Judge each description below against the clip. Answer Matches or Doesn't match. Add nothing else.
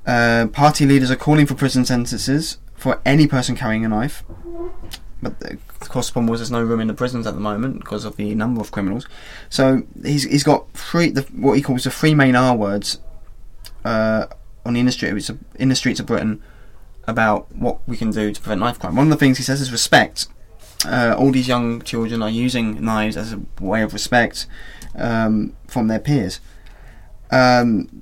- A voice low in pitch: Matches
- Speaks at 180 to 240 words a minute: Matches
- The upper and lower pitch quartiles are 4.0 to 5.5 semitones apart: Doesn't match